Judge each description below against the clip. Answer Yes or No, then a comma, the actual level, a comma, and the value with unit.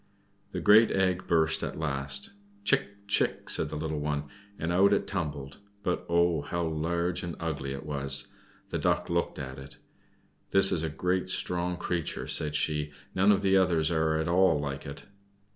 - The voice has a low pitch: Yes, very low, 80 Hz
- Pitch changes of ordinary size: Yes, average, 3.5 semitones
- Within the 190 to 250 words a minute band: No, average, 175 wpm